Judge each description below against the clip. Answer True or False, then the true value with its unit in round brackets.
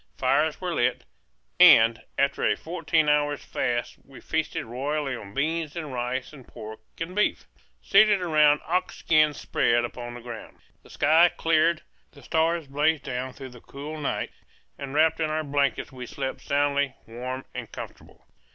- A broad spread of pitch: False (3.8 semitones)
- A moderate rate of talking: True (160 wpm)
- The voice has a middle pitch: True (145 Hz)